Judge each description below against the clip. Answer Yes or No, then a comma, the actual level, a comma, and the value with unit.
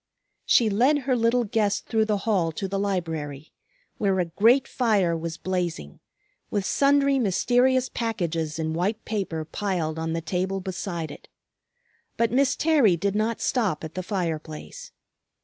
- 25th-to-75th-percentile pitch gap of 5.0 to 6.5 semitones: Yes, wide, 5.6 semitones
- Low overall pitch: No, high, 195 Hz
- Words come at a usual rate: Yes, average, 155 wpm